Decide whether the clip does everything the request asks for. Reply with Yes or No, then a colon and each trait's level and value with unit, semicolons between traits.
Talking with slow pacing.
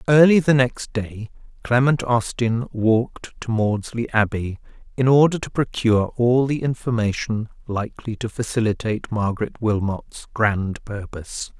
Yes: slow, 125 wpm